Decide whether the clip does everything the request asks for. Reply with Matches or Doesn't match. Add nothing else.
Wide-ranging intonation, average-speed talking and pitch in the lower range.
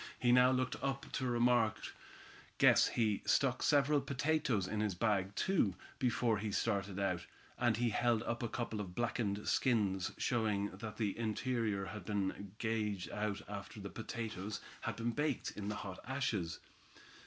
Doesn't match